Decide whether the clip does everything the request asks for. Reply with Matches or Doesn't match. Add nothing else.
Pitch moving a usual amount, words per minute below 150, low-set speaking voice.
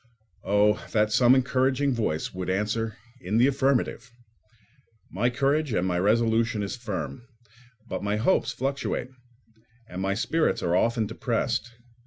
Matches